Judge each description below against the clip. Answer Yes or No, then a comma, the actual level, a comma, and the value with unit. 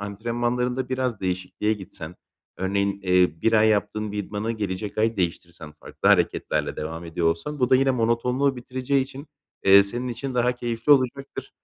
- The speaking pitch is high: No, low, 110 Hz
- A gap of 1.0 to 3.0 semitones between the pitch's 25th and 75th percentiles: No, average, 4.7 semitones